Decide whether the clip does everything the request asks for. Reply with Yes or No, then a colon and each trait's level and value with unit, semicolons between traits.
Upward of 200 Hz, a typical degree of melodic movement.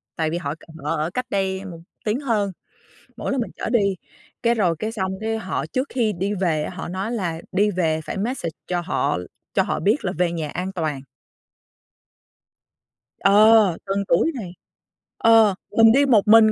No: high, 195 Hz; average, 4.4 semitones